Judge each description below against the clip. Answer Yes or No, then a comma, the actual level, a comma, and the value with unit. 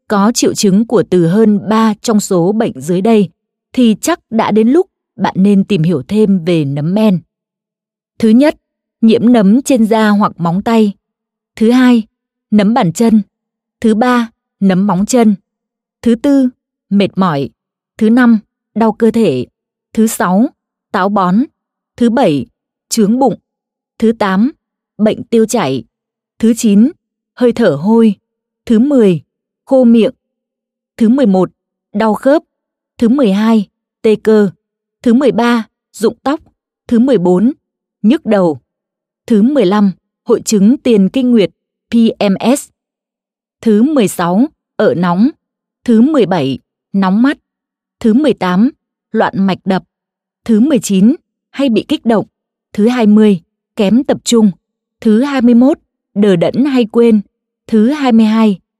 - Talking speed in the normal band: No, slow, 135 wpm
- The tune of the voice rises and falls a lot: No, average, 2.7 semitones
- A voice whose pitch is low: No, high, 225 Hz